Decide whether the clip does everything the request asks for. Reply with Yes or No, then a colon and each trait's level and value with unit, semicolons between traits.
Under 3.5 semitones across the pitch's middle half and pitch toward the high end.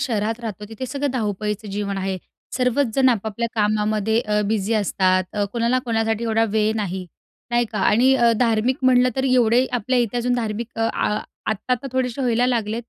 Yes: average, 2.8 semitones; high, 225 Hz